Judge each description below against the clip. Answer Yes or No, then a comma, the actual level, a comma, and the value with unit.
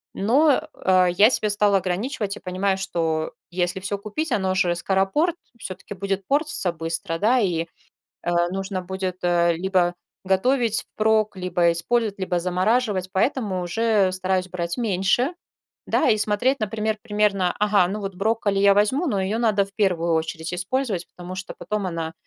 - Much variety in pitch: No, average, 2.9 semitones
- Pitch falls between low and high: No, high, 195 Hz